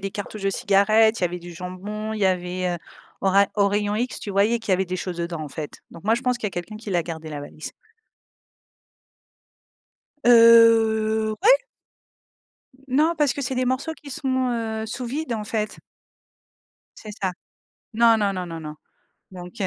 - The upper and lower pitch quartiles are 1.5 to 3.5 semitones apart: No, average, 4.1 semitones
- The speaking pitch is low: No, high, 210 Hz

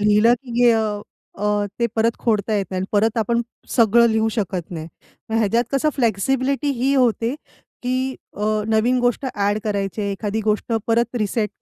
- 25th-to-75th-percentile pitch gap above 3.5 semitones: No, average, 2.7 semitones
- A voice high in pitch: Yes, high, 220 Hz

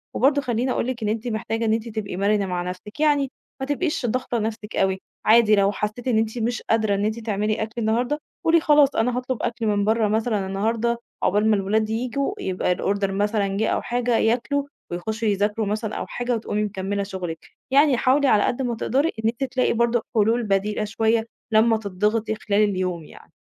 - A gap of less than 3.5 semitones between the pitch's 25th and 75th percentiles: Yes, average, 2.8 semitones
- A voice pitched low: No, high, 220 Hz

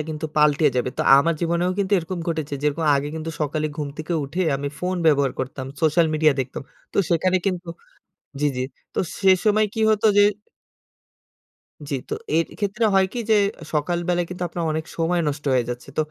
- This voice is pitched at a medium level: Yes, medium, 160 Hz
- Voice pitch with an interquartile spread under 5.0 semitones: Yes, average, 3.5 semitones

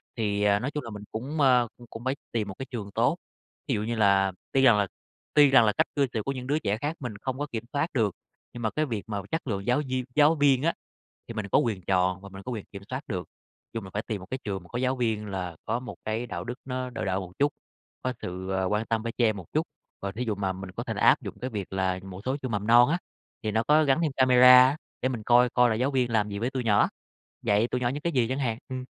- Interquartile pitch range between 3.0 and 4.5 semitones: Yes, average, 4.1 semitones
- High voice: No, low, 115 Hz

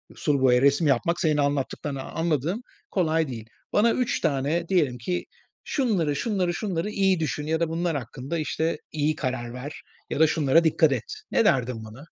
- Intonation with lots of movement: No, average, 4.0 semitones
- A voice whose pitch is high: No, medium, 155 Hz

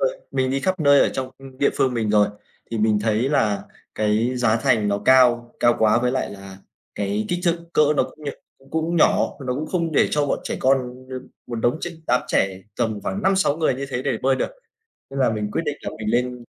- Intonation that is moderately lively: Yes, average, 4.4 semitones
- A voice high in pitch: No, low, 125 Hz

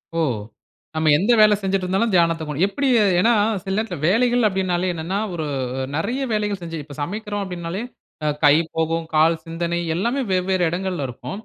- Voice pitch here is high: No, medium, 180 Hz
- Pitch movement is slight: No, average, 3.9 semitones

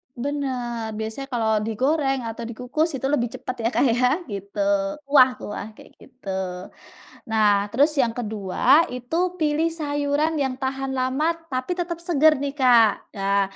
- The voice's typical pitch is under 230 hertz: No, very high, 255 Hz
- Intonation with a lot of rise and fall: No, average, 4.3 semitones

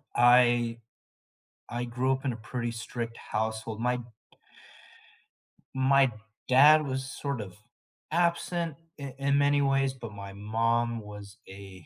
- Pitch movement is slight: No, average, 3.5 semitones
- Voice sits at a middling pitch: No, low, 120 Hz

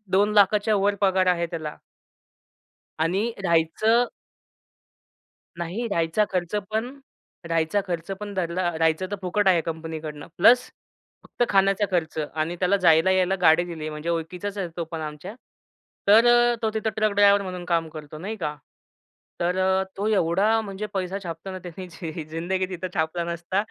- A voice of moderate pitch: Yes, medium, 180 Hz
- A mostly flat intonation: No, average, 3.6 semitones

